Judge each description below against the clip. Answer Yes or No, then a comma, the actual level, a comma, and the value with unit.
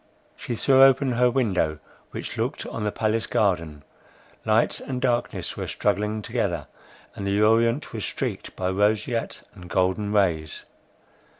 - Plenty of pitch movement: No, average, 4.2 semitones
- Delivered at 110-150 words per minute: Yes, average, 140 wpm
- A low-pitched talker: Yes, low, 105 Hz